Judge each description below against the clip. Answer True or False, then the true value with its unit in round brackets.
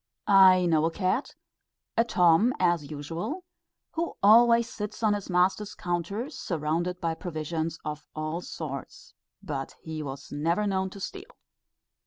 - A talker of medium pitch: True (180 Hz)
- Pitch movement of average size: True (4.6 semitones)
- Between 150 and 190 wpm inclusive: False (140 wpm)